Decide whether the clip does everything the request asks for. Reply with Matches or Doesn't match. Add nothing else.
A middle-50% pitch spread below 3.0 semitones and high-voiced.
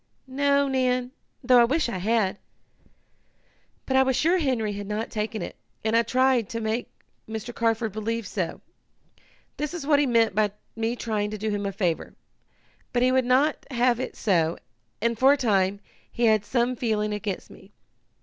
Doesn't match